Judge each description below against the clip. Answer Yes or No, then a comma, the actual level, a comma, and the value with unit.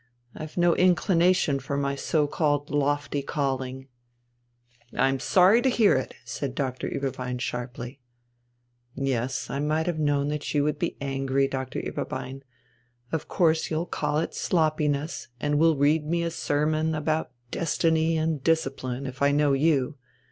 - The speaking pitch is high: No, medium, 145 Hz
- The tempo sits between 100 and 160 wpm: Yes, average, 150 wpm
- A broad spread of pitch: No, average, 2.8 semitones